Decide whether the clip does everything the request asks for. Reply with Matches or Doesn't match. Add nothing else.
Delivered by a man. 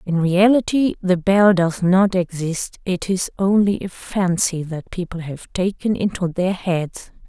Doesn't match